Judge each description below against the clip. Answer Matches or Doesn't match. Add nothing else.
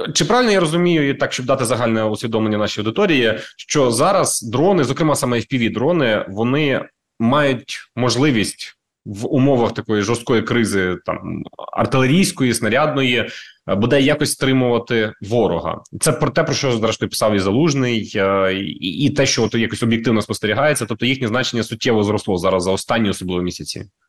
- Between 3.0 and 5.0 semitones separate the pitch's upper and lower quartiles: Matches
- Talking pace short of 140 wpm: Doesn't match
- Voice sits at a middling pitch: Doesn't match